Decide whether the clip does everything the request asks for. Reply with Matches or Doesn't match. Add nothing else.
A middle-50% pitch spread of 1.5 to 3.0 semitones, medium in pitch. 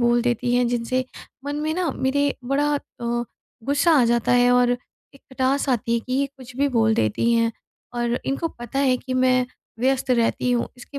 Doesn't match